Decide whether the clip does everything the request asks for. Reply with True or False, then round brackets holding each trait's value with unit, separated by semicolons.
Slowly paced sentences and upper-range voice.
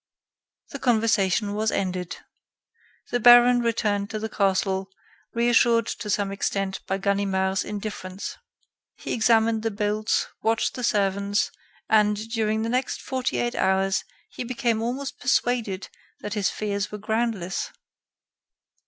True (125 wpm; 215 Hz)